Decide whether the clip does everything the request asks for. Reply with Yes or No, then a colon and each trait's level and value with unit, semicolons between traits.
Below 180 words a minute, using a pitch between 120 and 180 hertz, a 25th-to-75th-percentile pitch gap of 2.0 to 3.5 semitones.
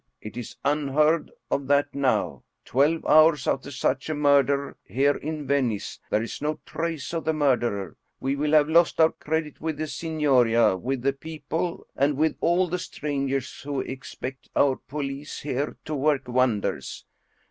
Yes: average, 160 wpm; medium, 140 Hz; narrow, 2.6 semitones